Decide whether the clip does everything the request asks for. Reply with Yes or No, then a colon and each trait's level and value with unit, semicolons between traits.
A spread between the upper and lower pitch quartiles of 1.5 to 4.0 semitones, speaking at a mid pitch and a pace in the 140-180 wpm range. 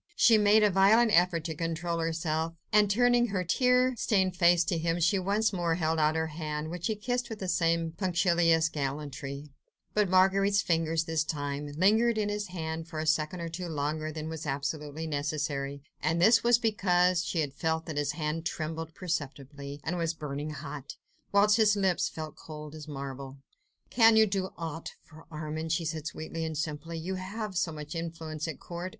No: average, 3.4 semitones; medium, 165 Hz; average, 190 wpm